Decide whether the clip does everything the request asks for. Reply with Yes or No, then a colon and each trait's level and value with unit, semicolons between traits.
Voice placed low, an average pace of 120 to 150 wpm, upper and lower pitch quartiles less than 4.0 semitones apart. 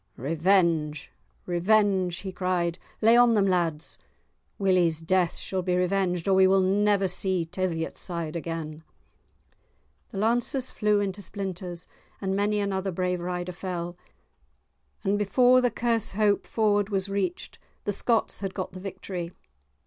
No: high, 190 Hz; slow, 135 wpm; narrow, 2.6 semitones